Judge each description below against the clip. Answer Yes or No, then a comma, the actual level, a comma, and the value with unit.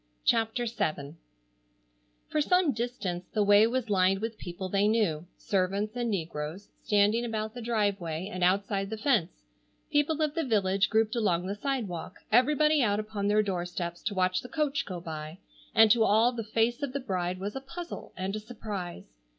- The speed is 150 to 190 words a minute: Yes, average, 175 wpm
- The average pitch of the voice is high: Yes, high, 210 Hz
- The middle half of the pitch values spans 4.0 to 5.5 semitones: Yes, average, 4.4 semitones